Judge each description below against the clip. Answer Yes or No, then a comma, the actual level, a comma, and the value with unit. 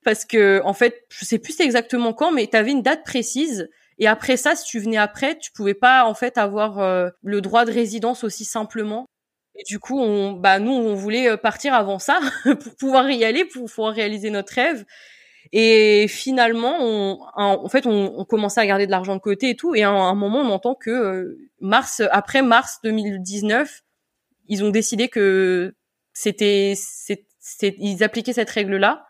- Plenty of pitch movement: No, average, 3.4 semitones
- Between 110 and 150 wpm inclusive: No, average, 195 wpm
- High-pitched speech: Yes, high, 220 Hz